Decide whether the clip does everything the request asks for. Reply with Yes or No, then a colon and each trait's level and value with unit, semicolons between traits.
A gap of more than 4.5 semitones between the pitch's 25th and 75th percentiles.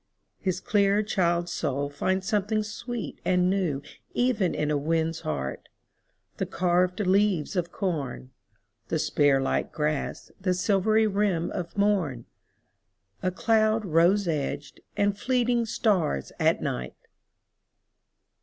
Yes: average, 5.2 semitones